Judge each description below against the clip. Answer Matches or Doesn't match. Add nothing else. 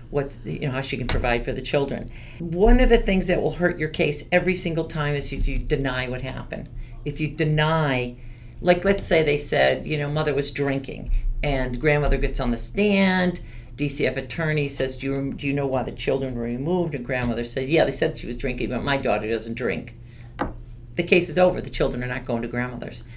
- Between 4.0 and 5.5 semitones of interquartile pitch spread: Matches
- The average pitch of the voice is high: Doesn't match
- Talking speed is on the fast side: Matches